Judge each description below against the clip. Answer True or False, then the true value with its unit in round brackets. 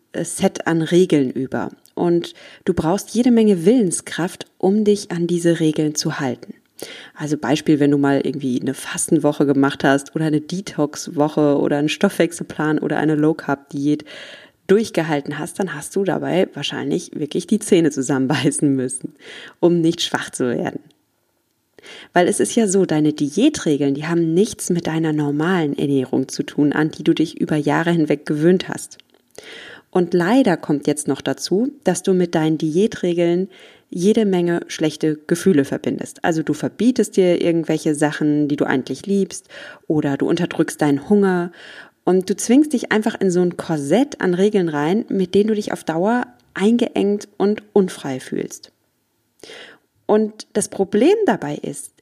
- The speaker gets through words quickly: False (160 wpm)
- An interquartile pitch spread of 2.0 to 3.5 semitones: False (4.6 semitones)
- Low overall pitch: False (170 Hz)